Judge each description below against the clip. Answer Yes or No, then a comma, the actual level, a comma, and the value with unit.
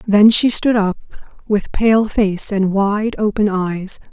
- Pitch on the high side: Yes, high, 205 Hz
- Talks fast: No, average, 160 wpm